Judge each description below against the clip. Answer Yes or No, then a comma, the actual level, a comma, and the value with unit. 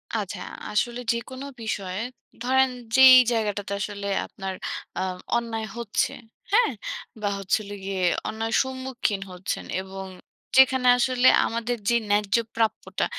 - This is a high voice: Yes, high, 225 Hz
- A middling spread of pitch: Yes, average, 4.1 semitones